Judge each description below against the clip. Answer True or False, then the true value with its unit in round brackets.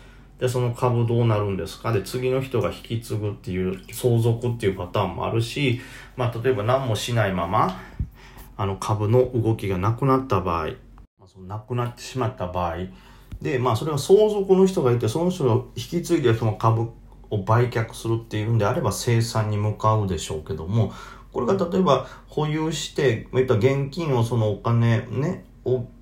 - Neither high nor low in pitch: False (120 Hz)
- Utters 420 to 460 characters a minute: False (365 characters per minute)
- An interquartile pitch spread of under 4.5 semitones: True (3.1 semitones)